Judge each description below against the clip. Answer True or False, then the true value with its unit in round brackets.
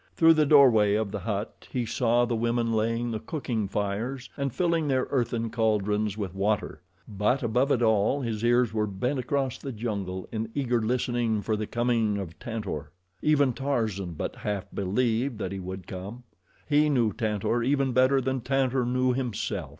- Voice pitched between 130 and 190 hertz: False (115 Hz)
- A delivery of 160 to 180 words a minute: True (175 wpm)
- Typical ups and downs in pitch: True (3.5 semitones)